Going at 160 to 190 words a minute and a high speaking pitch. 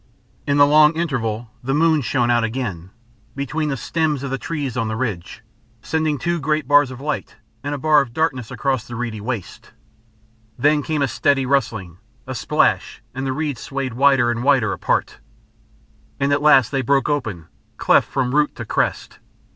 No: average, 180 wpm; low, 135 Hz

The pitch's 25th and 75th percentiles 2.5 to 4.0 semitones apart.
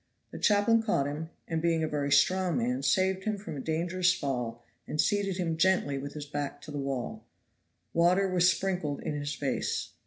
No: average, 4.5 semitones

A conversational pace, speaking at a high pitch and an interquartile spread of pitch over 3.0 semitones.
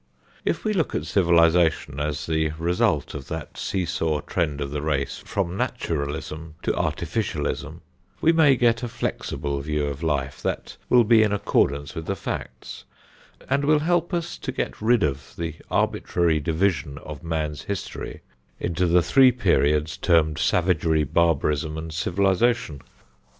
No: average, 150 wpm; very low, 80 Hz; average, 4.8 semitones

